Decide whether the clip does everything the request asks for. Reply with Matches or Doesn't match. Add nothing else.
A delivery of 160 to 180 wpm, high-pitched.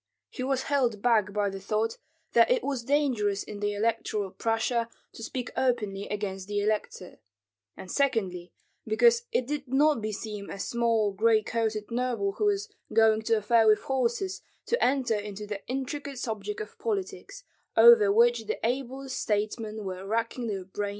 Matches